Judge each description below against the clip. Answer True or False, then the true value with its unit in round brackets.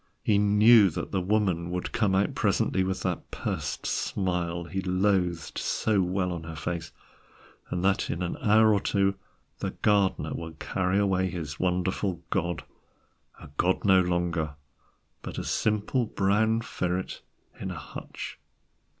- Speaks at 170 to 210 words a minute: False (150 wpm)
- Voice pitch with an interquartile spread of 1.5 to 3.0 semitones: True (2.5 semitones)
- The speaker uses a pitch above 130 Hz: False (95 Hz)